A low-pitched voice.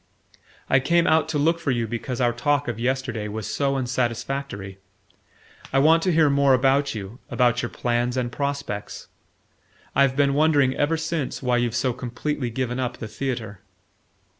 Yes: low, 130 Hz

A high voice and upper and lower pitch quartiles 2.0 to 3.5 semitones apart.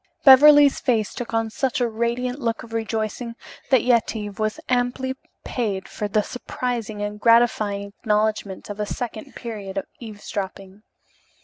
Yes: high, 225 Hz; average, 2.8 semitones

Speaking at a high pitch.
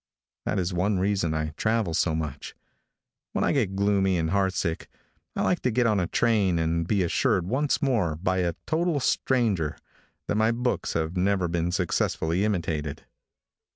No: very low, 95 Hz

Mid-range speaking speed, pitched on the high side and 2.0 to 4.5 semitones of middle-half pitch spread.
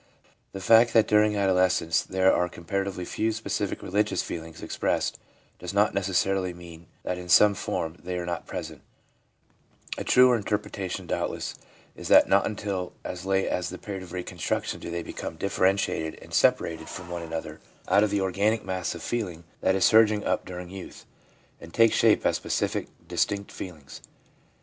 No: average, 170 wpm; very low, 95 Hz; narrow, 2.5 semitones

